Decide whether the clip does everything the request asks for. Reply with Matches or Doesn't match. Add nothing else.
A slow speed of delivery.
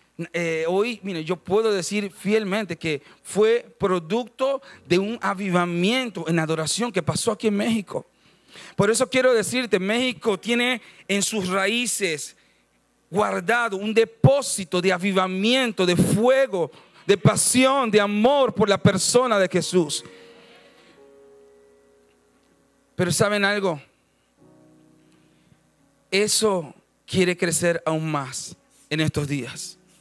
Matches